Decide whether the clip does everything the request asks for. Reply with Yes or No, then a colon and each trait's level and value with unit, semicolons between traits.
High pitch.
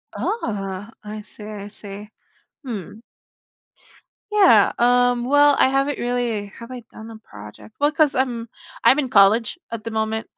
Yes: high, 230 Hz